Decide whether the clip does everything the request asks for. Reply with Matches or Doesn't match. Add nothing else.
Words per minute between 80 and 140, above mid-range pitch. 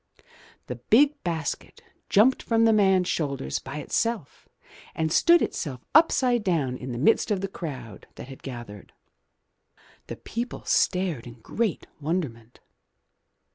Doesn't match